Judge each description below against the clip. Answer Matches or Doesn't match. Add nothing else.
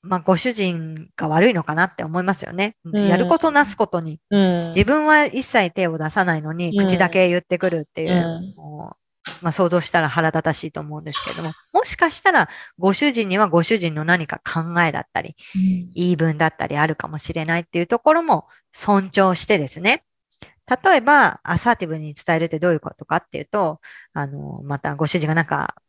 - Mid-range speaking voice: Matches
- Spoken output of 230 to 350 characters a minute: Doesn't match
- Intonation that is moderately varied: Matches